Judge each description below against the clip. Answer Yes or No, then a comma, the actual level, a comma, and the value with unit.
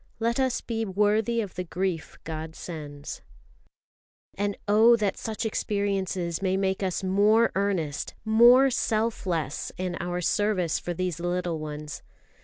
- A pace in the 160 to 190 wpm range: No, average, 140 wpm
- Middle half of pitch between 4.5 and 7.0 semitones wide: No, average, 3.9 semitones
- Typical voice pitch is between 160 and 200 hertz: Yes, high, 190 Hz